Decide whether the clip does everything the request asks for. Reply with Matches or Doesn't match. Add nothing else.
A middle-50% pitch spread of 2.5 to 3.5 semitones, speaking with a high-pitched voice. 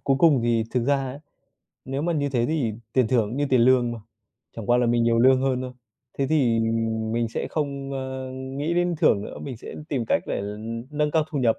Doesn't match